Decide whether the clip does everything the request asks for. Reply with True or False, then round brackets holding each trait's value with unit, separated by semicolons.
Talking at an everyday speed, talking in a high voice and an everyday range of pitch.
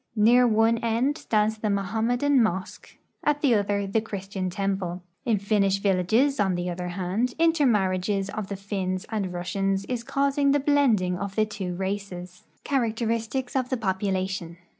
True (160 wpm; 205 Hz; 3.8 semitones)